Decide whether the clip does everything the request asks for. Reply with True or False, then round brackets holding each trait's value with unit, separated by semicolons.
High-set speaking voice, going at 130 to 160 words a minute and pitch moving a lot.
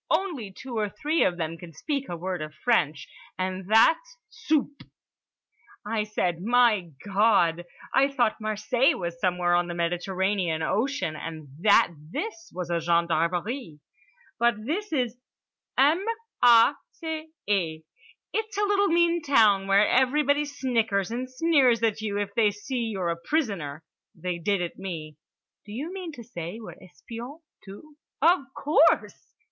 True (215 Hz; 150 wpm; 7.7 semitones)